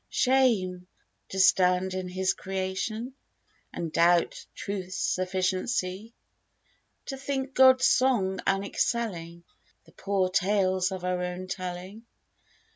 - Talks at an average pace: No, slow, 105 wpm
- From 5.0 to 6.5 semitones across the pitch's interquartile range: No, average, 3.3 semitones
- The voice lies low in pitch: No, high, 190 Hz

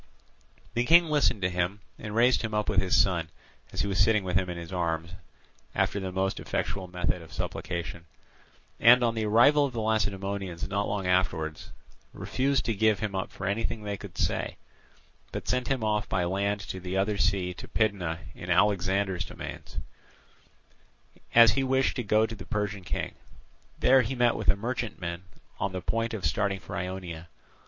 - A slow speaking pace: No, average, 185 wpm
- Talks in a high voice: No, low, 100 Hz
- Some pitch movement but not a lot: Yes, average, 3.5 semitones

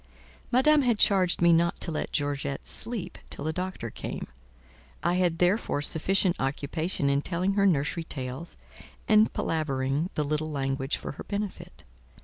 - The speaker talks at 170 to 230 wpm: No, average, 150 wpm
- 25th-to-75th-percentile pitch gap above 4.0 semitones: Yes, average, 4.7 semitones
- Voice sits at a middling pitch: Yes, medium, 165 Hz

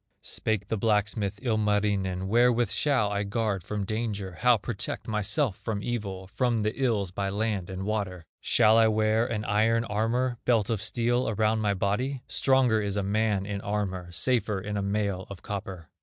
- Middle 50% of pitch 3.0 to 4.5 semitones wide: No, narrow, 2.4 semitones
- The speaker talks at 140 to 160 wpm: No, average, 170 wpm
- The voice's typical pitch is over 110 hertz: No, low, 105 Hz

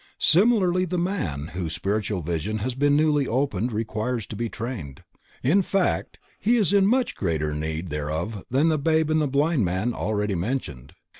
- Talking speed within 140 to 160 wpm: No, average, 170 wpm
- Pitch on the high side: No, low, 115 Hz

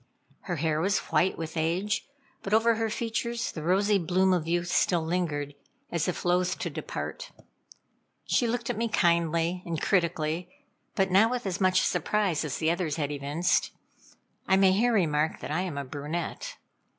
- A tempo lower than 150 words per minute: No, average, 175 wpm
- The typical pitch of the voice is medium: Yes, medium, 175 Hz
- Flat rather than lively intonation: No, average, 3.7 semitones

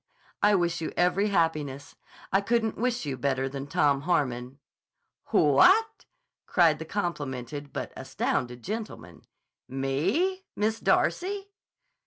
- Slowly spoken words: Yes, slow, 115 wpm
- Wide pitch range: Yes, wide, 7.6 semitones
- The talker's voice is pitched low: No, medium, 160 Hz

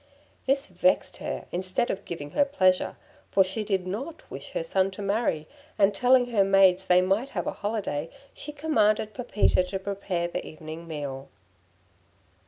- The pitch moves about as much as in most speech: Yes, average, 4.5 semitones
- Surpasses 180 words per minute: No, average, 165 wpm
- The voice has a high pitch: Yes, high, 195 Hz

